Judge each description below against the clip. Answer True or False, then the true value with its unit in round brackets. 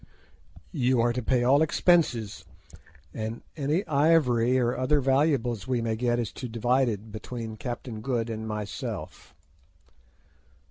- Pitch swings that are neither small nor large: True (3.1 semitones)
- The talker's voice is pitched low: True (120 Hz)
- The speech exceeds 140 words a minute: False (135 wpm)